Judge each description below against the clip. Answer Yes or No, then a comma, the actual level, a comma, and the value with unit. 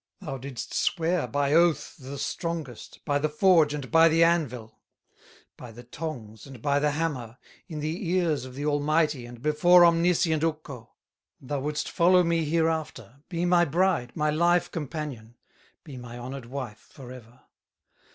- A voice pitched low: No, medium, 150 Hz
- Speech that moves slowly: No, average, 155 wpm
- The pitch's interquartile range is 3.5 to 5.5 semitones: Yes, average, 4.4 semitones